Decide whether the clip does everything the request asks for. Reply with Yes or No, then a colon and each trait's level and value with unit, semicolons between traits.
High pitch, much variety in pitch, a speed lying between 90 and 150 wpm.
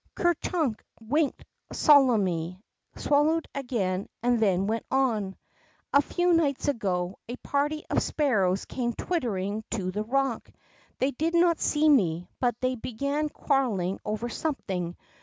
Yes: high, 245 Hz; wide, 6.7 semitones; slow, 135 wpm